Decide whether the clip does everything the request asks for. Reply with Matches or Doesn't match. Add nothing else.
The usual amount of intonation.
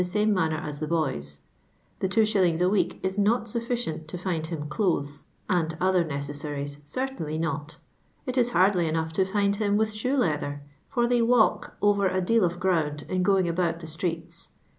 Matches